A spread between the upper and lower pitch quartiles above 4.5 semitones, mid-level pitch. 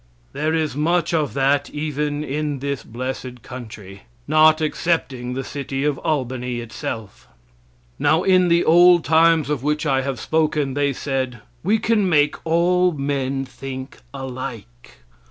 No: average, 3.3 semitones; medium, 145 Hz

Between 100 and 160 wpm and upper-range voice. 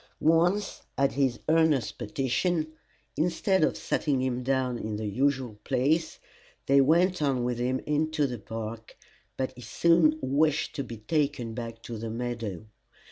No: average, 150 wpm; low, 130 Hz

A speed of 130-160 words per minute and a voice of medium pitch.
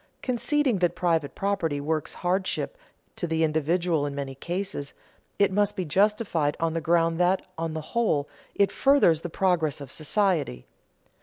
Yes: average, 155 wpm; medium, 170 Hz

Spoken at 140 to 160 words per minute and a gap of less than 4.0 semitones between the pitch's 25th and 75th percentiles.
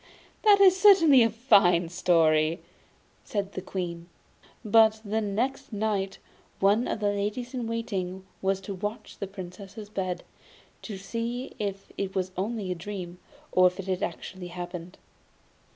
Yes: average, 150 wpm; average, 3.4 semitones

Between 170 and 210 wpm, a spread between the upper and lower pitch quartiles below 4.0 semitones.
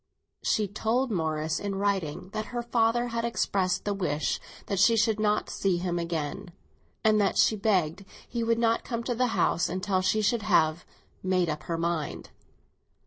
No: average, 175 wpm; average, 4.5 semitones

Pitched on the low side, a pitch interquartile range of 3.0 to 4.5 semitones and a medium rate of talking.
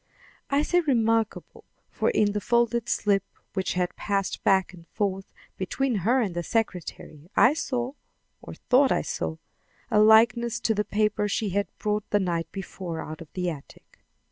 No: high, 210 Hz; average, 4.1 semitones; average, 170 wpm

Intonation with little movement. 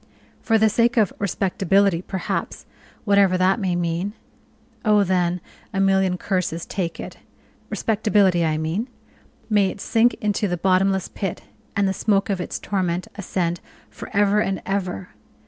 Yes: narrow, 2.2 semitones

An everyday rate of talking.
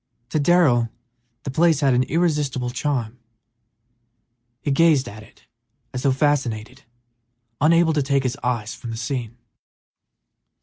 No: slow, 130 wpm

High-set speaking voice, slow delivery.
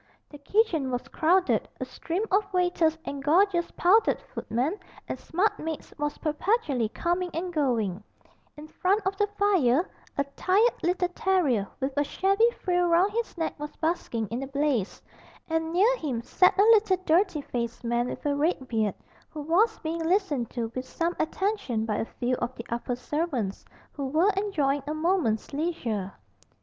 No: very high, 320 Hz; average, 170 wpm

